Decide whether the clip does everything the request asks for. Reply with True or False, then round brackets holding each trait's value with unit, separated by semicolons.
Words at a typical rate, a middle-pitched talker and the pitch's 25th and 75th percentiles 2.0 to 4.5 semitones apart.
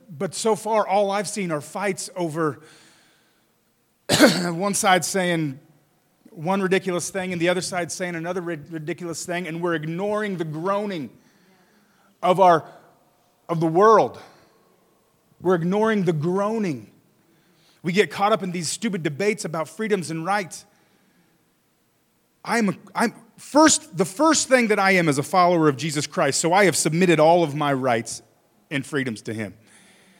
True (155 wpm; 180 Hz; 3.6 semitones)